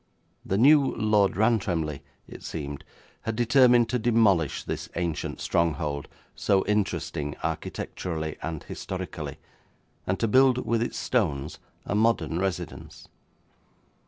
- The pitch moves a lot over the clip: Yes, wide, 6.3 semitones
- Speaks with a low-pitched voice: Yes, very low, 95 Hz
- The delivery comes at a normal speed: No, slow, 115 wpm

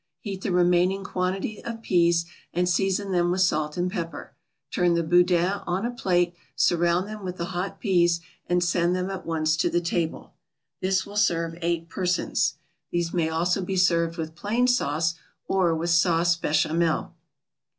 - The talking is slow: No, average, 170 wpm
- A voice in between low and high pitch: Yes, medium, 175 Hz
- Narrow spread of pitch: Yes, narrow, 2.0 semitones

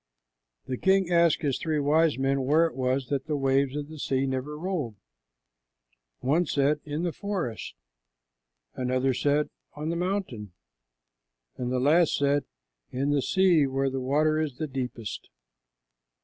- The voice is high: No, medium, 145 Hz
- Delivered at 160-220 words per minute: No, average, 150 wpm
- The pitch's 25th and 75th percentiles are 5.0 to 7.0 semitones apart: No, average, 3.2 semitones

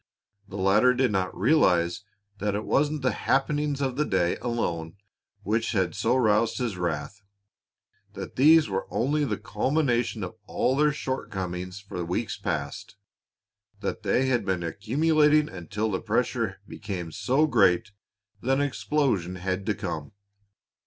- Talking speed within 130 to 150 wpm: Yes, average, 145 wpm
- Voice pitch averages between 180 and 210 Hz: No, low, 110 Hz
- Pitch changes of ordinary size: No, wide, 6.4 semitones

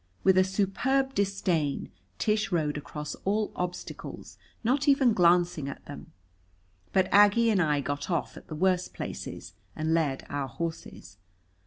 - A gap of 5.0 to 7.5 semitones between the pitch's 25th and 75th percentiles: Yes, average, 5.3 semitones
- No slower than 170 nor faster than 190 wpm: No, average, 145 wpm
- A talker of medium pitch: Yes, medium, 180 Hz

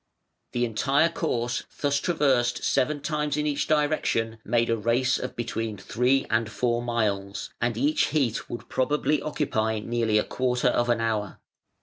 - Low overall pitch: Yes, low, 120 Hz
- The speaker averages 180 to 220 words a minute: No, average, 155 wpm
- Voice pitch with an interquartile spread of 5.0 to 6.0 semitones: No, average, 4.0 semitones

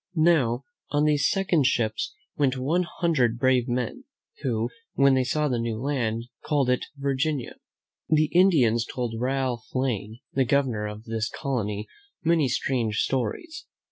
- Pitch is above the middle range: No, low, 130 Hz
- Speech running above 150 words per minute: No, average, 140 wpm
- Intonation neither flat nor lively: Yes, average, 4.0 semitones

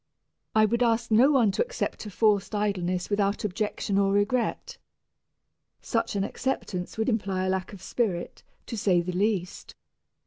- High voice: Yes, high, 205 Hz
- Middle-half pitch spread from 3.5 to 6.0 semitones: No, average, 3.0 semitones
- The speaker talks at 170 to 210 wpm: No, average, 160 wpm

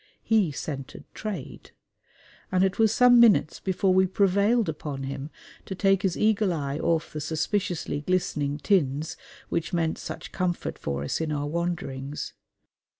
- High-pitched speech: No, medium, 170 Hz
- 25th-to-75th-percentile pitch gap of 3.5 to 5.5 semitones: Yes, average, 4.9 semitones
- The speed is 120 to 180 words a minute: Yes, average, 150 wpm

